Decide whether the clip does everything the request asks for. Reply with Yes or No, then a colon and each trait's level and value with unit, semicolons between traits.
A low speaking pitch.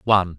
Yes: very low, 95 Hz